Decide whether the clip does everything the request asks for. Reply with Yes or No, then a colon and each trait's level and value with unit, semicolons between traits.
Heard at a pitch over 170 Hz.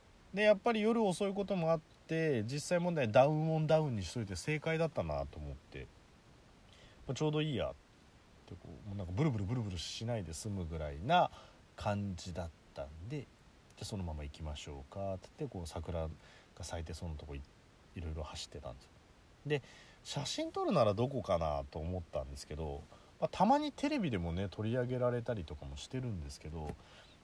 No: low, 100 Hz